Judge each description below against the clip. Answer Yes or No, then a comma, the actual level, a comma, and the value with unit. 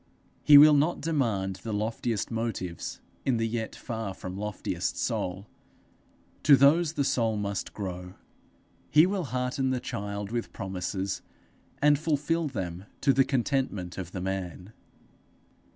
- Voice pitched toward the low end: Yes, low, 115 Hz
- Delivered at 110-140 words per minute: Yes, slow, 135 wpm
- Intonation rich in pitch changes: Yes, wide, 6.3 semitones